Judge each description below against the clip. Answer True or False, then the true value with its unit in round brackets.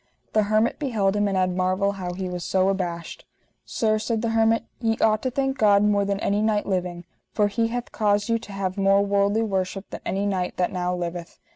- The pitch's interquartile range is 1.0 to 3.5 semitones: True (2.7 semitones)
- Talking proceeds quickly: True (220 wpm)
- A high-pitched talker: True (200 Hz)